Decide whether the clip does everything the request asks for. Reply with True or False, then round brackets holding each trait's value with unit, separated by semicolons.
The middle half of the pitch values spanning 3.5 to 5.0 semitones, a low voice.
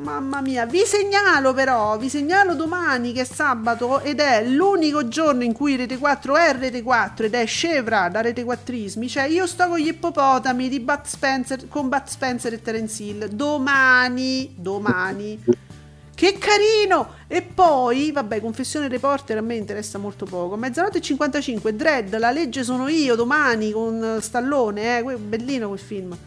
False (4.6 semitones; 260 Hz)